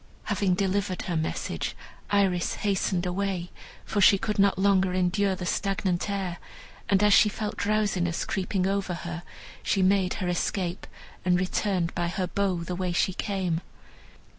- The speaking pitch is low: No, high, 190 Hz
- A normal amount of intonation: No, narrow, 2.0 semitones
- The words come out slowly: No, average, 155 wpm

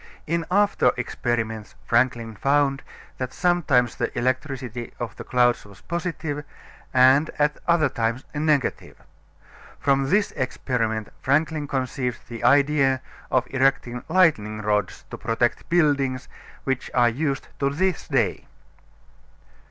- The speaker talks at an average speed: No, slow, 120 wpm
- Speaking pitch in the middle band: No, low, 130 Hz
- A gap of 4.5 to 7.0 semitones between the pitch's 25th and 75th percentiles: No, average, 3.6 semitones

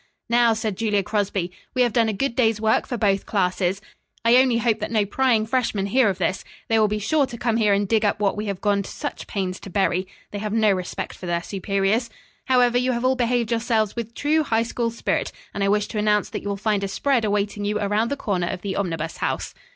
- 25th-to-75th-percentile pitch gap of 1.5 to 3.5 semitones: Yes, average, 2.8 semitones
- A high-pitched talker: Yes, high, 215 Hz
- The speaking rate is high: Yes, fast, 245 wpm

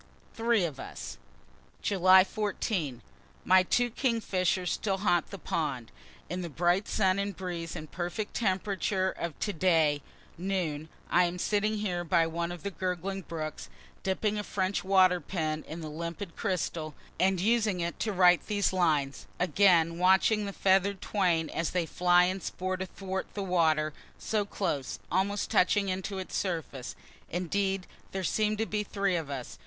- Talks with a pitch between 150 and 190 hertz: Yes, medium, 185 Hz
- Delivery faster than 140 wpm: Yes, average, 160 wpm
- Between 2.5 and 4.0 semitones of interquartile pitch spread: Yes, average, 2.8 semitones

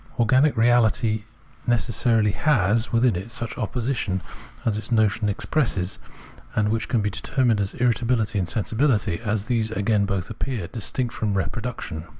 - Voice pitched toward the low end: Yes, low, 110 Hz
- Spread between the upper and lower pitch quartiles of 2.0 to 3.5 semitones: Yes, average, 2.8 semitones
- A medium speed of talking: Yes, average, 150 wpm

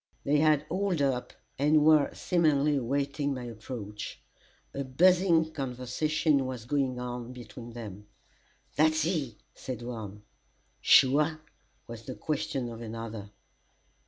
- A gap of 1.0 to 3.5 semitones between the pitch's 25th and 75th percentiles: No, average, 4.2 semitones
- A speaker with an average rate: No, slow, 120 wpm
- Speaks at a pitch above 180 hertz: No, low, 135 Hz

